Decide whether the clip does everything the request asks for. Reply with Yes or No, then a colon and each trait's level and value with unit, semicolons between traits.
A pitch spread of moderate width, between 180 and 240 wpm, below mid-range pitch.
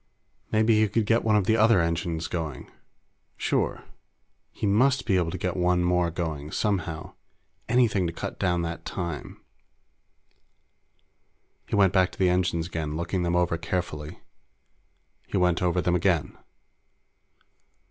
No: average, 3.1 semitones; average, 145 wpm; very low, 90 Hz